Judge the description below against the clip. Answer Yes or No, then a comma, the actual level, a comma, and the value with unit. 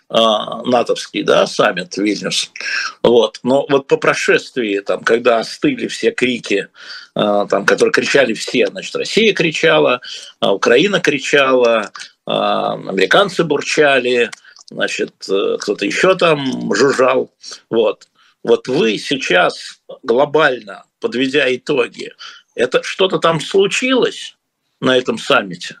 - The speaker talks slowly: Yes, slow, 100 wpm